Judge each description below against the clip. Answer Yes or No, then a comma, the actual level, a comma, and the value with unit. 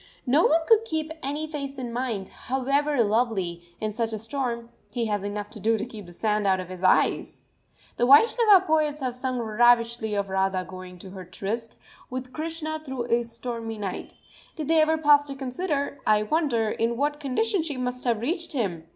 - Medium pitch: No, high, 245 Hz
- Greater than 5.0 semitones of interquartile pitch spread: Yes, wide, 5.5 semitones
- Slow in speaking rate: No, average, 195 wpm